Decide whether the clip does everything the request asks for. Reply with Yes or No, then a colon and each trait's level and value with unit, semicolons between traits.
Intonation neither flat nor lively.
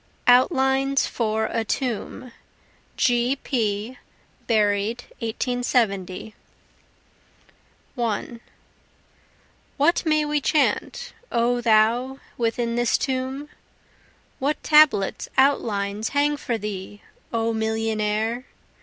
Yes: average, 3.4 semitones